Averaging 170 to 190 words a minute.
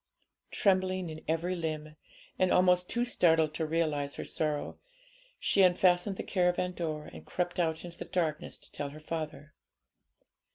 No: average, 155 wpm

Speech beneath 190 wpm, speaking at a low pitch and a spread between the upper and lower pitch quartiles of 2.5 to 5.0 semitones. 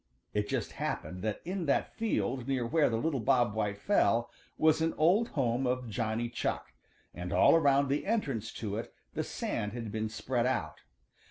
Yes: average, 180 wpm; low, 120 Hz; average, 4.7 semitones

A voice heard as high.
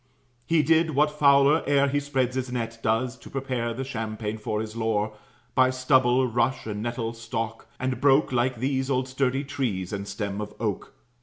No: low, 125 Hz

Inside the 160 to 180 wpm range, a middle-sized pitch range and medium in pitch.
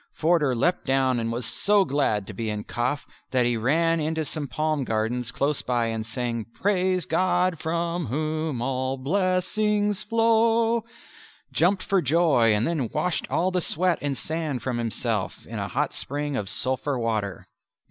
No: average, 165 wpm; wide, 6.6 semitones; medium, 145 Hz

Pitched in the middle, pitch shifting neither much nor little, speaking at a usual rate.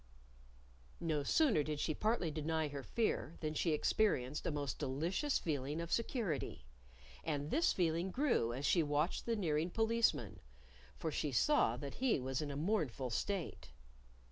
No: medium, 160 Hz; wide, 5.9 semitones; average, 155 wpm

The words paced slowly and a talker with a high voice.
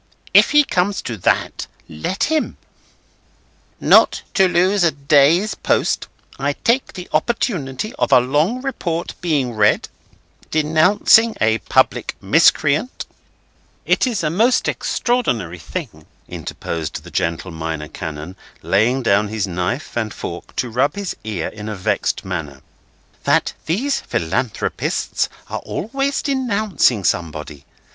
No: slow, 125 wpm; medium, 140 Hz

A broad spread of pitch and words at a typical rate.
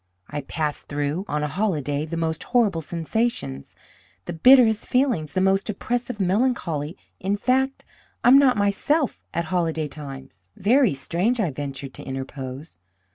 Yes: wide, 7.4 semitones; average, 145 wpm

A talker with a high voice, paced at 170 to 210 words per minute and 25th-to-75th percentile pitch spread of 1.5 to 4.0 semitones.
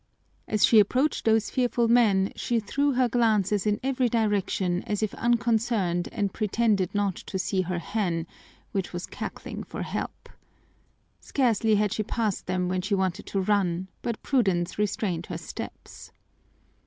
No: high, 210 Hz; average, 155 wpm; average, 3.7 semitones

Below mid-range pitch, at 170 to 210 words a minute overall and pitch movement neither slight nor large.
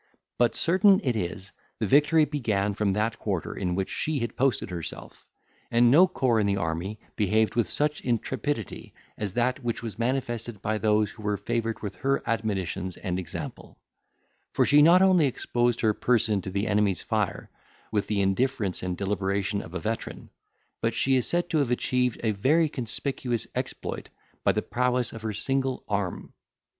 Yes: low, 115 Hz; average, 175 wpm; average, 4.2 semitones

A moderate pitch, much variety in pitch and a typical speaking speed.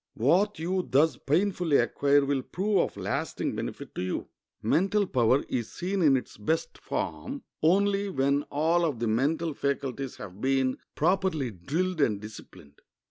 Yes: medium, 145 Hz; wide, 5.7 semitones; average, 150 wpm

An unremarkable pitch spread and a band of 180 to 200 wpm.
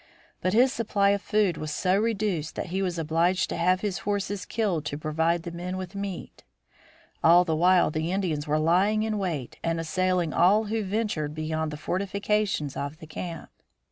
Yes: average, 3.9 semitones; average, 185 wpm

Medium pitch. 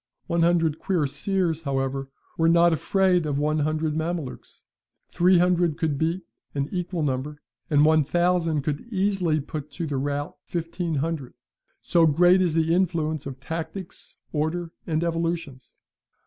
Yes: medium, 160 Hz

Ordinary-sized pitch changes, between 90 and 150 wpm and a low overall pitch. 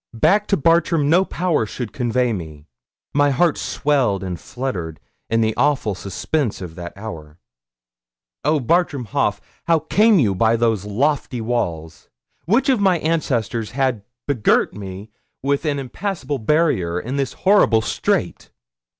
No: wide, 7.0 semitones; average, 140 wpm; low, 125 Hz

